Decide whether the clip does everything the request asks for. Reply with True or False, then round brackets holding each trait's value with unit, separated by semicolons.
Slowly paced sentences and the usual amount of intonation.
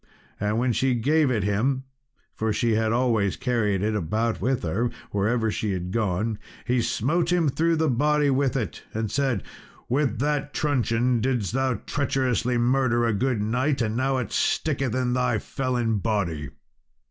False (165 wpm; 3.5 semitones)